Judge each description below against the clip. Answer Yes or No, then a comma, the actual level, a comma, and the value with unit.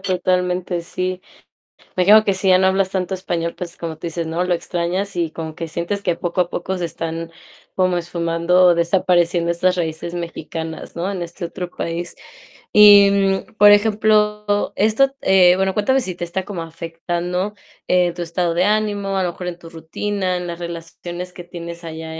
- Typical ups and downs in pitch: No, narrow, 2.1 semitones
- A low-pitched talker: No, medium, 180 Hz